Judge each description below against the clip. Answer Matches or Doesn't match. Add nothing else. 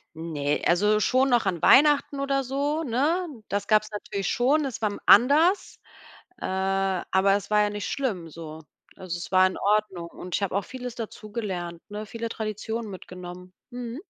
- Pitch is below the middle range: Doesn't match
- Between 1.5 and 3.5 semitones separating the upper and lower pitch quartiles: Doesn't match